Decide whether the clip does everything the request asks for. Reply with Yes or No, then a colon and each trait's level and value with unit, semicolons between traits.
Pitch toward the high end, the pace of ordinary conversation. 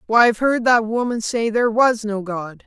No: high, 225 Hz; fast, 225 wpm